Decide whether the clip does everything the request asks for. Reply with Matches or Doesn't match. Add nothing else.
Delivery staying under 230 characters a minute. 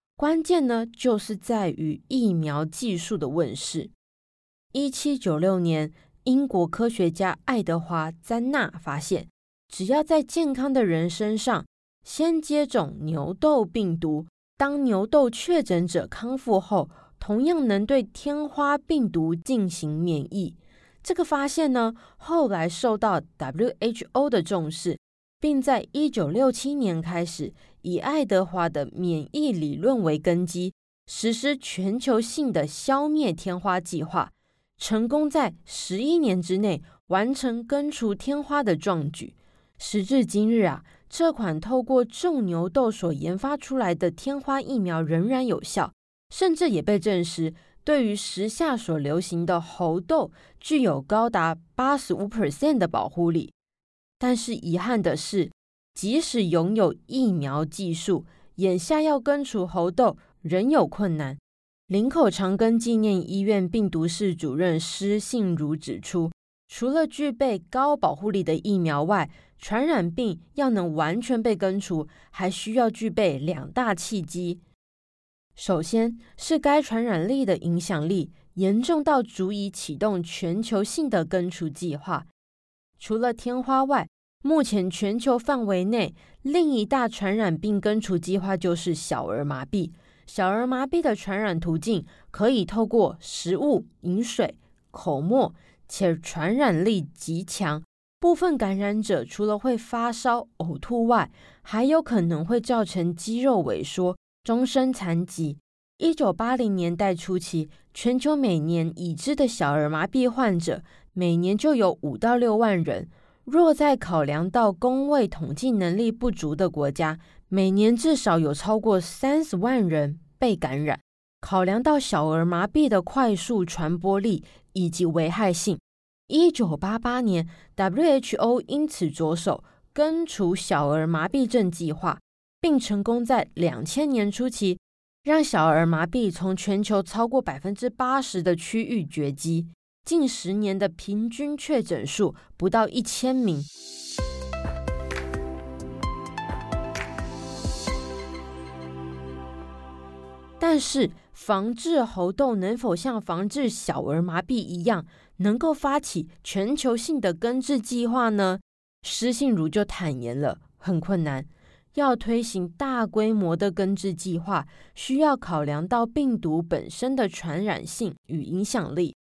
Matches